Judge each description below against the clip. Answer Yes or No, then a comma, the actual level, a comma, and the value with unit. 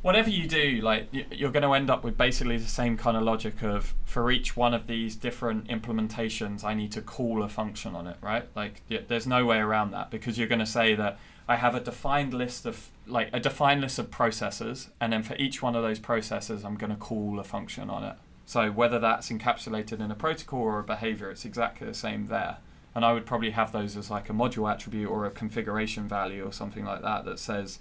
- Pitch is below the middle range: Yes, low, 115 Hz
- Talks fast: Yes, fast, 235 wpm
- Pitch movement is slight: Yes, narrow, 2.3 semitones